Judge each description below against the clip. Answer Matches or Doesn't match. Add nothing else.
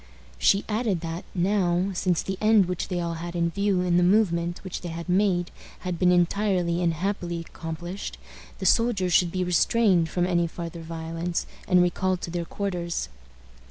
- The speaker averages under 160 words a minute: Doesn't match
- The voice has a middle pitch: Matches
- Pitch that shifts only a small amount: Matches